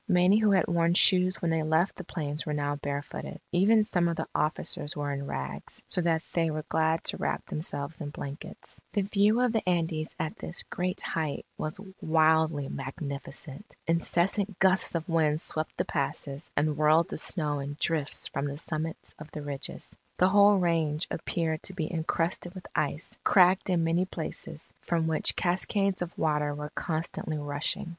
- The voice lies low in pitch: No, medium, 160 Hz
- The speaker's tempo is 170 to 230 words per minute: Yes, average, 180 wpm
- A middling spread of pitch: Yes, average, 3.1 semitones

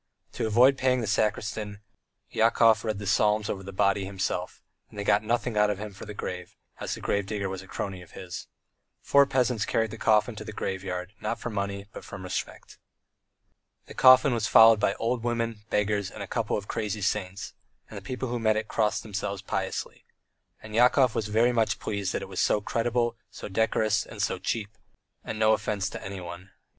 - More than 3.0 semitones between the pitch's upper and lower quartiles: No, narrow, 2.4 semitones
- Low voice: Yes, low, 105 Hz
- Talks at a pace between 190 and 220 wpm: Yes, average, 200 wpm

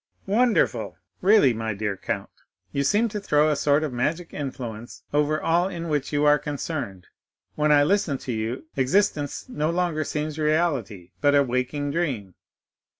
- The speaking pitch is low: No, medium, 150 Hz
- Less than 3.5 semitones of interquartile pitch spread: No, average, 4.5 semitones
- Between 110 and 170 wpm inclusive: Yes, average, 160 wpm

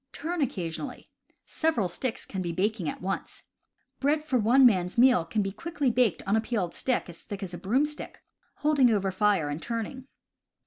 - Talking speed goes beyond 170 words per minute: Yes, average, 185 wpm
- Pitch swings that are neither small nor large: No, wide, 5.8 semitones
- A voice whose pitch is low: No, high, 220 Hz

